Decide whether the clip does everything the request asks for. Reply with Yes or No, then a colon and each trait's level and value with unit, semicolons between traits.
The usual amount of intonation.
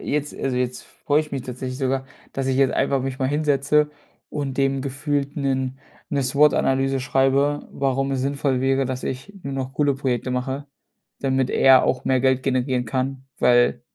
No: narrow, 1.2 semitones